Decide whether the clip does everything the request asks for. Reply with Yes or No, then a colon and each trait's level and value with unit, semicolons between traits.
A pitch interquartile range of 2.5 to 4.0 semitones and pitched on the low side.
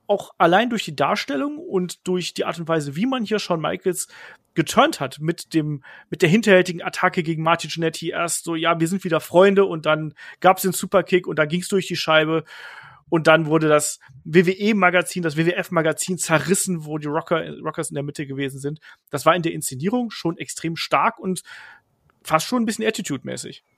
No: average, 2.9 semitones; medium, 170 Hz